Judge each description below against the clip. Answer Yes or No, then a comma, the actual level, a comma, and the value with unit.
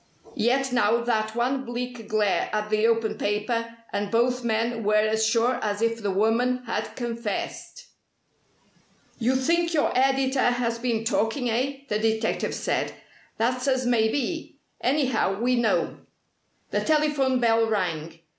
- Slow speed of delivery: No, average, 145 wpm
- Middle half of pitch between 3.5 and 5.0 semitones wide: No, narrow, 2.5 semitones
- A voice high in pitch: Yes, high, 235 Hz